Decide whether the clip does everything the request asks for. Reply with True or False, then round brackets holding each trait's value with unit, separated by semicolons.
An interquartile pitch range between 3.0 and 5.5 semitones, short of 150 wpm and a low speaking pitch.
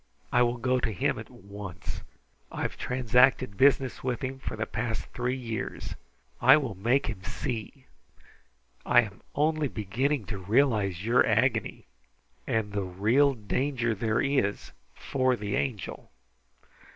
True (4.1 semitones; 140 wpm; 120 Hz)